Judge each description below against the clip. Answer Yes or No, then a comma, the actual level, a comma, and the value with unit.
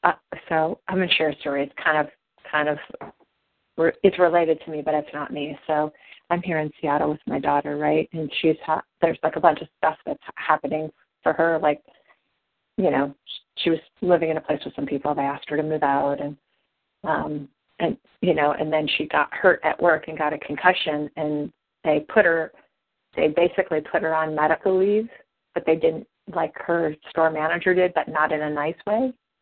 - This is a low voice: No, medium, 155 Hz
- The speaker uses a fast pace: Yes, fast, 210 wpm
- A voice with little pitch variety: Yes, narrow, 2.0 semitones